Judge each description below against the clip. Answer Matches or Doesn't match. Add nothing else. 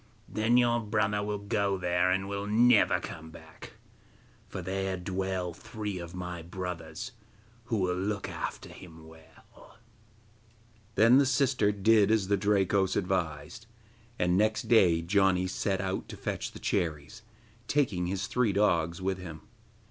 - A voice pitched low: Matches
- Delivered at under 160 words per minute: Matches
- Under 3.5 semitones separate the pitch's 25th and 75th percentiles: Matches